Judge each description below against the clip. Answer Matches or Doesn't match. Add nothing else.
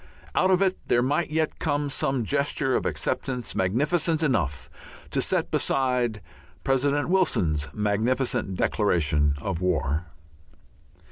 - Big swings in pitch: Matches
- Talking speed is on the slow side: Matches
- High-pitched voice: Doesn't match